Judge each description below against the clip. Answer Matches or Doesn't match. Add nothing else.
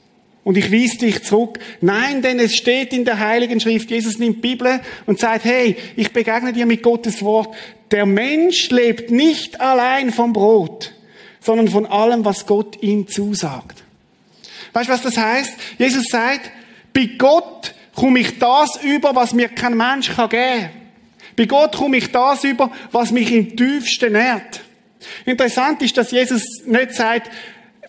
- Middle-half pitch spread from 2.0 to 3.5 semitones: Matches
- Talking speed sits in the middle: Matches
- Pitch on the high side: Matches